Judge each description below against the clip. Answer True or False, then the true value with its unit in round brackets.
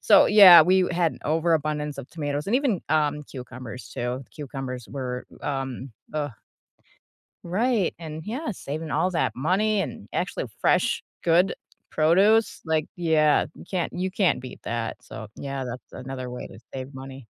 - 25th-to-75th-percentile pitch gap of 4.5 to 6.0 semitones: True (5.2 semitones)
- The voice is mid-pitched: True (155 Hz)